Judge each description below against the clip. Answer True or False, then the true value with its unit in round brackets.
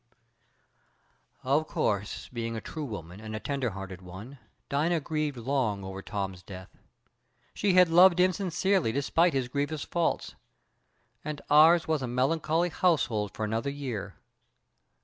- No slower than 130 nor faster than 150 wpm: True (140 wpm)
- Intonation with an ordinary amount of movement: False (6.8 semitones)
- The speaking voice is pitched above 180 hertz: False (140 Hz)